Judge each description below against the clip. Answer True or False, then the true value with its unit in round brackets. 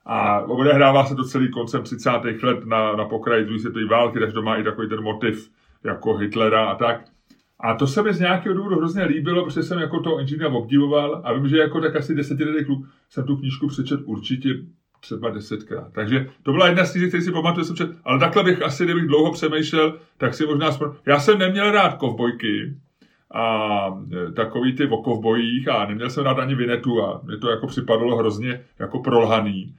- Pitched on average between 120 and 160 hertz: True (135 Hz)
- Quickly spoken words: True (195 wpm)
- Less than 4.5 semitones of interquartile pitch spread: False (5.4 semitones)